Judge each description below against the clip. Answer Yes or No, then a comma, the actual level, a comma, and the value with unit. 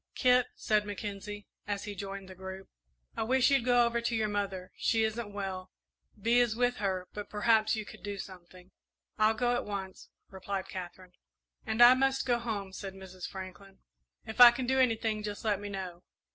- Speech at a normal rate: Yes, average, 190 wpm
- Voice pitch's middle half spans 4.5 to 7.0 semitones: No, average, 3.5 semitones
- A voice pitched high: Yes, high, 205 Hz